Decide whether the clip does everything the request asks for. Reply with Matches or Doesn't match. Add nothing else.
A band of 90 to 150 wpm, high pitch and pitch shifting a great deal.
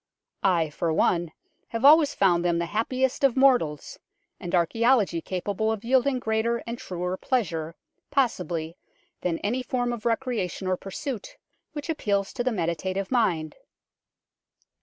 Matches